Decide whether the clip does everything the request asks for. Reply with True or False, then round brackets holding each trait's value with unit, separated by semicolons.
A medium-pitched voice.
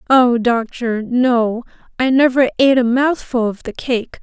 False (245 Hz)